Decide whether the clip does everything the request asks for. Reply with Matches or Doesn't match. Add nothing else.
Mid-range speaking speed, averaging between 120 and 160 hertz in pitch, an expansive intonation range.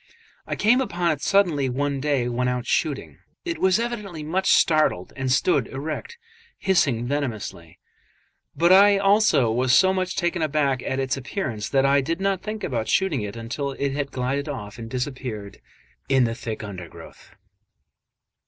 Matches